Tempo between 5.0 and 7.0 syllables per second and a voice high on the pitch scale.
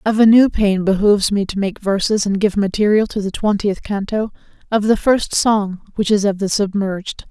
Yes: 5.1 syllables/s; high, 205 Hz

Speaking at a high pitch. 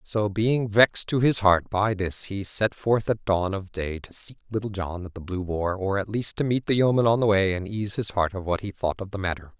No: low, 100 Hz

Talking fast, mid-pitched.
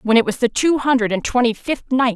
No: fast, 280 wpm; high, 245 Hz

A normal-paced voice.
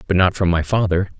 No: fast, 250 wpm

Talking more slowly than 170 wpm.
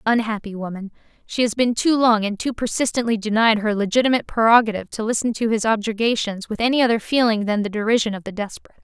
No: average, 195 wpm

